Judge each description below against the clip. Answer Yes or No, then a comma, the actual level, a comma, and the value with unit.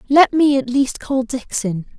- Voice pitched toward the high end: Yes, very high, 255 Hz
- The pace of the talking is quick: No, average, 180 wpm